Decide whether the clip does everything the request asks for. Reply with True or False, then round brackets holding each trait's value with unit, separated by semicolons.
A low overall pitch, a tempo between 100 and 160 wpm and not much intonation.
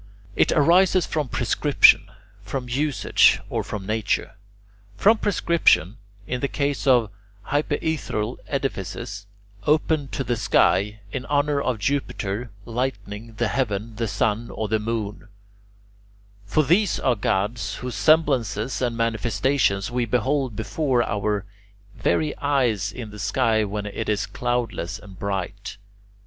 False (115 Hz; 135 wpm; 4.8 semitones)